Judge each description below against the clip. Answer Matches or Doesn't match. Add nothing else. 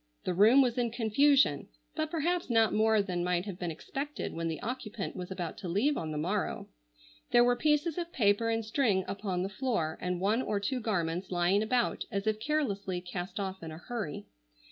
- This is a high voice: Matches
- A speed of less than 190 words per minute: Doesn't match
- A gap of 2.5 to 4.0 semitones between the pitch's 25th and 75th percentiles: Doesn't match